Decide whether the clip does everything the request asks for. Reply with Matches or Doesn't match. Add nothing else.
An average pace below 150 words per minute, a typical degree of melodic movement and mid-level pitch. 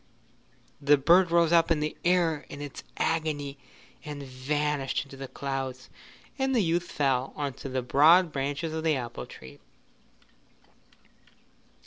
Matches